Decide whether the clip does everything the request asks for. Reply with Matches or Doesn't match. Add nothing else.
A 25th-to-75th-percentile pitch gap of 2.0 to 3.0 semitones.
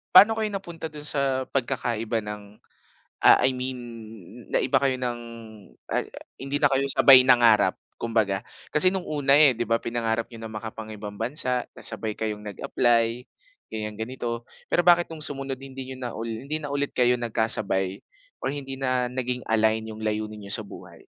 Doesn't match